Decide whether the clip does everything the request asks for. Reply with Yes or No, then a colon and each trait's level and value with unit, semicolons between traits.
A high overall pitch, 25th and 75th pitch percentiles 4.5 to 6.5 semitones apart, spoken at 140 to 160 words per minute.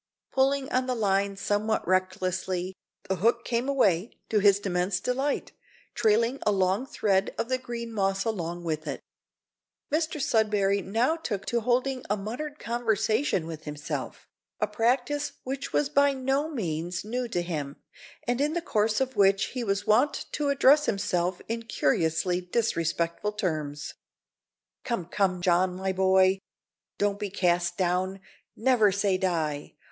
Yes: high, 205 Hz; average, 5.1 semitones; average, 150 wpm